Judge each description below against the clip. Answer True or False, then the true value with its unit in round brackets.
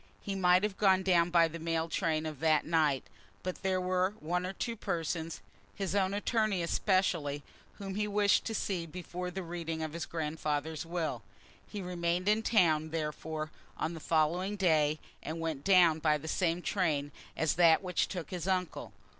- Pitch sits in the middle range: True (170 Hz)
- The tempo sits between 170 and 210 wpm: True (180 wpm)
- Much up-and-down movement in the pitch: False (2.9 semitones)